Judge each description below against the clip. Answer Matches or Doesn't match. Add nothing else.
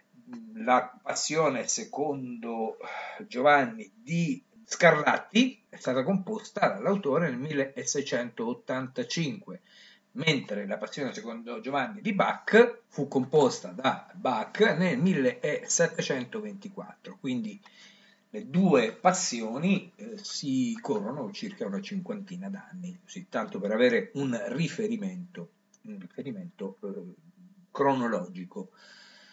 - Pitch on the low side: Doesn't match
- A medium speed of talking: Doesn't match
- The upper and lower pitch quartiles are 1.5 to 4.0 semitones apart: Doesn't match